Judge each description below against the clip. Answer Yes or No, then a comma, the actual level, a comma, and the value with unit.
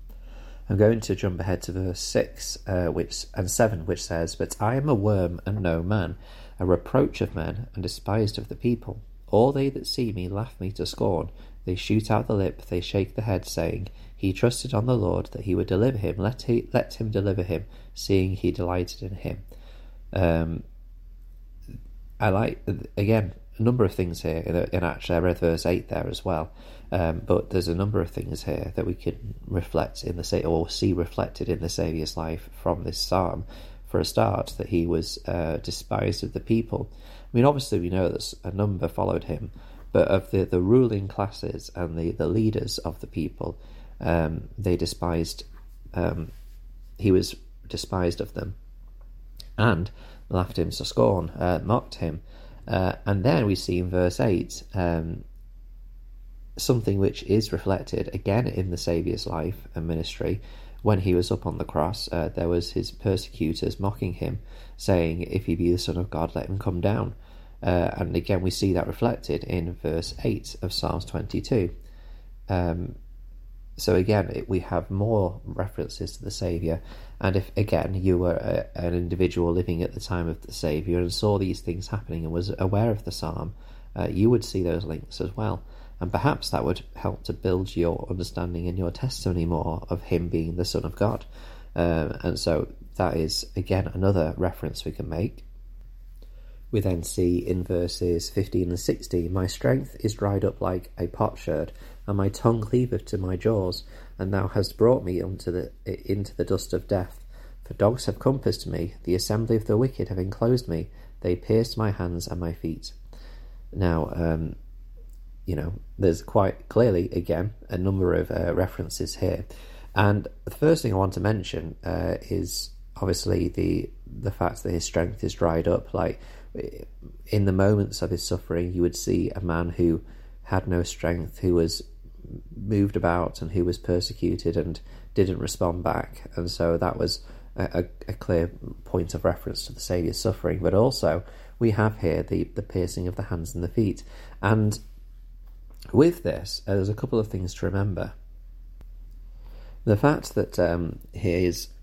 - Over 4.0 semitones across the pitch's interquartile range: No, average, 3.5 semitones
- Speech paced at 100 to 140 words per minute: No, average, 185 wpm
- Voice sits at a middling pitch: No, very low, 90 Hz